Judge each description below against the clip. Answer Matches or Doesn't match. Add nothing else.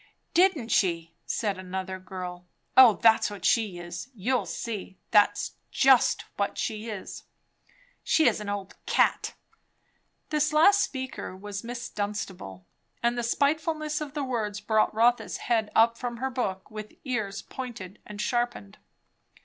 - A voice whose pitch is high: Matches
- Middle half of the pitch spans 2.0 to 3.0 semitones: Doesn't match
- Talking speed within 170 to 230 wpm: Doesn't match